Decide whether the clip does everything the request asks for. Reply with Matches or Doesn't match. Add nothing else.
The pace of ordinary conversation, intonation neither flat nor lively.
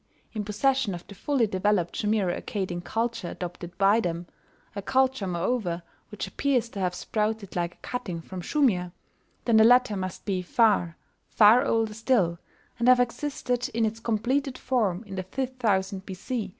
Matches